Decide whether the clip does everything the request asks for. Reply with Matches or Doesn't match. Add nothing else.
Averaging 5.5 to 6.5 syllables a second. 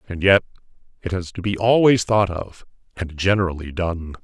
Doesn't match